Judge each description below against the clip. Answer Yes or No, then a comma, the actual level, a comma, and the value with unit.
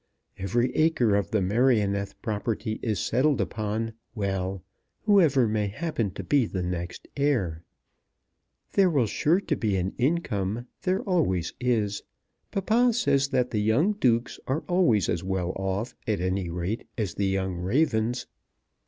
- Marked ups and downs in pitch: Yes, wide, 6.2 semitones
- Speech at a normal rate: Yes, average, 145 wpm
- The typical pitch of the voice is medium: No, low, 110 Hz